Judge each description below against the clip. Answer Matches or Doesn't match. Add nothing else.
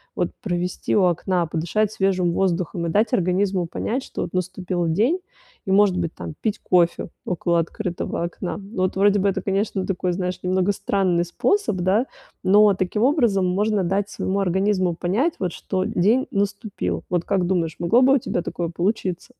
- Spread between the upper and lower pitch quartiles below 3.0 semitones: Matches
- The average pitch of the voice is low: Doesn't match